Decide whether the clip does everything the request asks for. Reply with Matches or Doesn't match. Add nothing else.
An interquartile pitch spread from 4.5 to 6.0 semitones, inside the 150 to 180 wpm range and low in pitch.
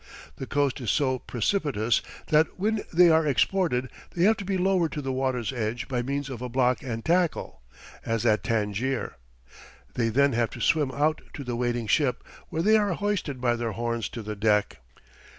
Doesn't match